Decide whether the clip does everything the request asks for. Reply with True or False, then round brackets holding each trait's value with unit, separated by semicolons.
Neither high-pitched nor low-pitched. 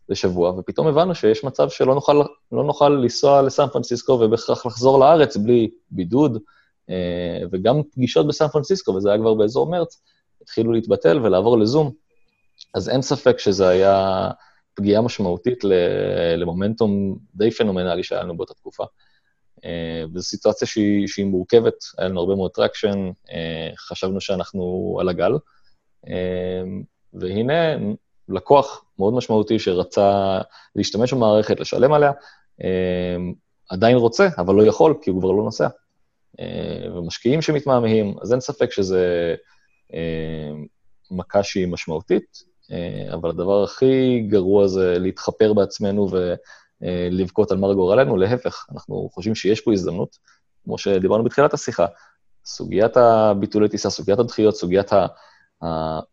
False (100 Hz)